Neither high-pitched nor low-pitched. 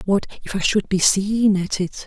No: high, 195 Hz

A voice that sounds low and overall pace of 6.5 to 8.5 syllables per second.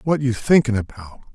Yes: low, 125 Hz; 6.6 syllables/s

